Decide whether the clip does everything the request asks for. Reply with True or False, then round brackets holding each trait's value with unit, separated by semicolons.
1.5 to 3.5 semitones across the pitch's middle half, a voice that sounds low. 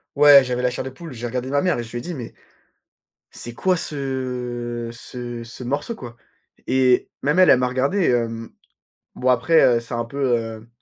True (2.7 semitones; 125 Hz)